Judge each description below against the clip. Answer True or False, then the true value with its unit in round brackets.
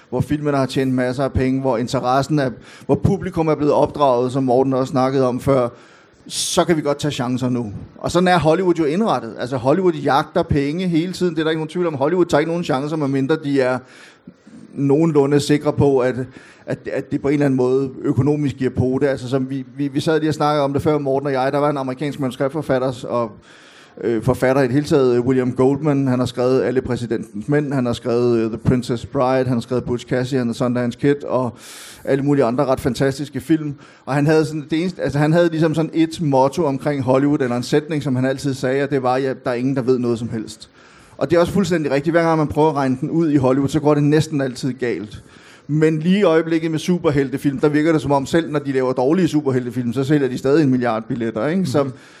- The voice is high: False (140 Hz)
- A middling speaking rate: False (240 wpm)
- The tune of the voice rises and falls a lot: False (2.9 semitones)